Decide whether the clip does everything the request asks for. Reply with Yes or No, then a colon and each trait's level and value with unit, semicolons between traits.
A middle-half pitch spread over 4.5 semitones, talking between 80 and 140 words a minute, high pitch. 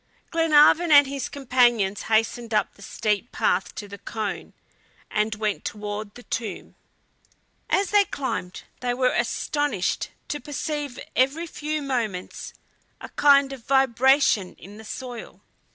Yes: average, 5.2 semitones; slow, 135 wpm; high, 245 Hz